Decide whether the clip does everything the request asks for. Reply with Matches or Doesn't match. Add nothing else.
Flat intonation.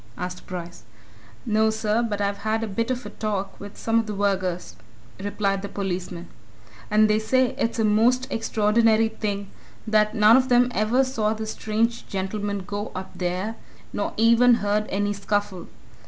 Matches